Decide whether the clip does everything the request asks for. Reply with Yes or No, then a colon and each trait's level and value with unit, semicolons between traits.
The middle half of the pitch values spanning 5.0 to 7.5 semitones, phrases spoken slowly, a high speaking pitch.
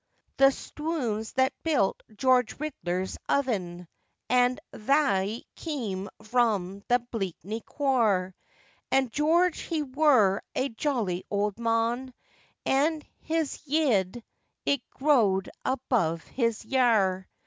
Yes: wide, 5.5 semitones; slow, 105 wpm; high, 240 Hz